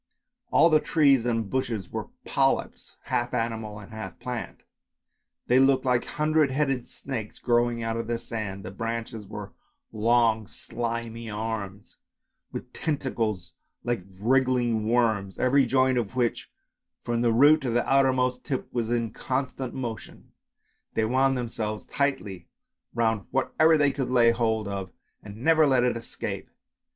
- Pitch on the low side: Yes, low, 120 Hz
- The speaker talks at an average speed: Yes, average, 145 wpm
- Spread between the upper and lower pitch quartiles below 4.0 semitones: Yes, average, 2.9 semitones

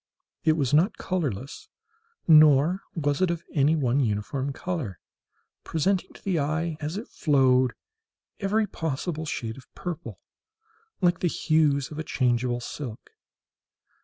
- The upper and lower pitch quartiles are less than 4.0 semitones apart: No, average, 4.3 semitones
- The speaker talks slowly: Yes, slow, 130 wpm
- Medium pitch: Yes, medium, 150 Hz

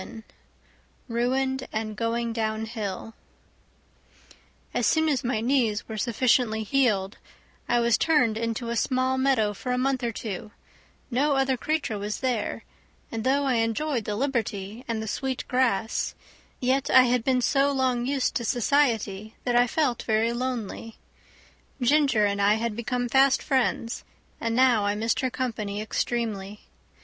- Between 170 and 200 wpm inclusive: No, average, 150 wpm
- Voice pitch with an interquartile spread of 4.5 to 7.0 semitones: No, average, 3.0 semitones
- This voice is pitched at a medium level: No, high, 235 Hz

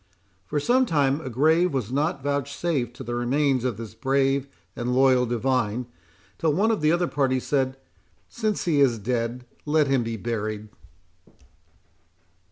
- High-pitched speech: No, low, 135 Hz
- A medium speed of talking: Yes, average, 155 wpm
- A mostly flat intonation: No, average, 3.7 semitones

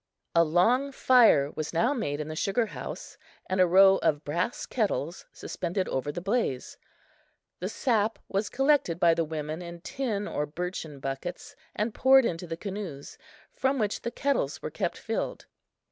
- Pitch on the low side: No, medium, 185 Hz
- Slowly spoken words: No, average, 165 wpm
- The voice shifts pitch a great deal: Yes, wide, 6.2 semitones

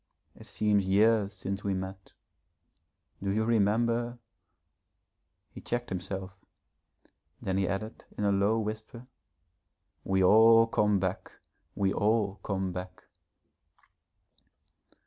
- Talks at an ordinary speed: No, slow, 110 wpm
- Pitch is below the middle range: Yes, low, 100 Hz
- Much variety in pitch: No, narrow, 2.4 semitones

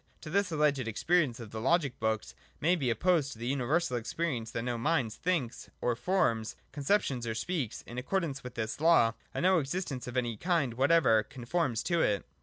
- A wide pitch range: Yes, wide, 6.2 semitones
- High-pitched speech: No, low, 135 Hz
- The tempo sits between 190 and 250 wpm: Yes, average, 200 wpm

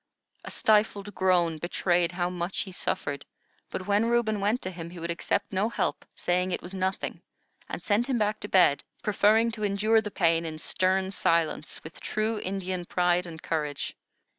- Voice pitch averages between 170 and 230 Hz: Yes, medium, 185 Hz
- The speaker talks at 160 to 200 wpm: Yes, average, 180 wpm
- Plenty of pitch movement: No, average, 3.3 semitones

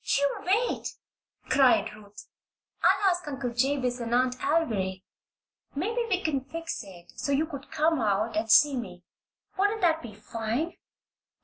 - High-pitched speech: Yes, very high, 270 Hz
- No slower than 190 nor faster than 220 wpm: No, average, 145 wpm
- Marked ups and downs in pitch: Yes, wide, 6.6 semitones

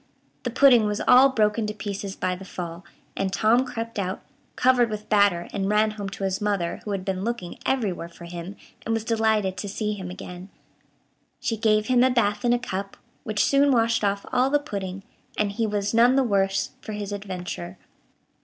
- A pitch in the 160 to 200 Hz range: No, high, 210 Hz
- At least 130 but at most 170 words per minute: No, average, 200 wpm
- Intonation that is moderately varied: Yes, average, 3.0 semitones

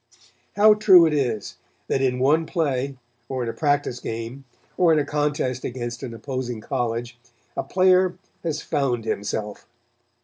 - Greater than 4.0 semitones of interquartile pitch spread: Yes, average, 4.4 semitones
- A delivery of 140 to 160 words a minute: Yes, average, 150 wpm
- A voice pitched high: No, low, 135 Hz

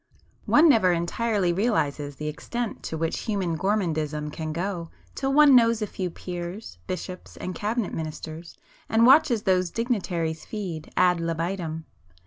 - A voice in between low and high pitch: Yes, medium, 180 Hz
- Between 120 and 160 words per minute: Yes, average, 140 wpm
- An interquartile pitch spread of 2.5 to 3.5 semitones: No, average, 4.9 semitones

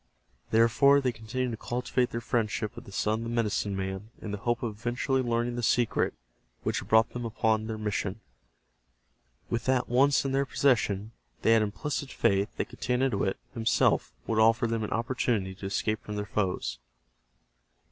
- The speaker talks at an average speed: Yes, average, 175 wpm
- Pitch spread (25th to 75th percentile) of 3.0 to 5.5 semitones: No, narrow, 2.5 semitones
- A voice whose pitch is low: Yes, low, 115 Hz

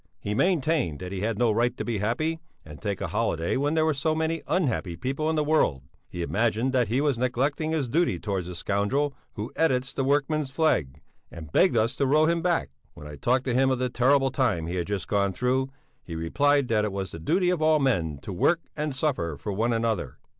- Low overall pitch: Yes, low, 125 Hz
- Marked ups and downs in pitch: Yes, wide, 6.9 semitones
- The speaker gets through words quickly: Yes, fast, 230 wpm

